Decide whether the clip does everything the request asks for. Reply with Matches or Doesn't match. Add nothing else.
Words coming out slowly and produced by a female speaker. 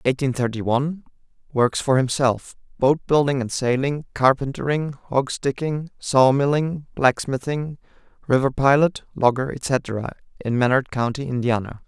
Doesn't match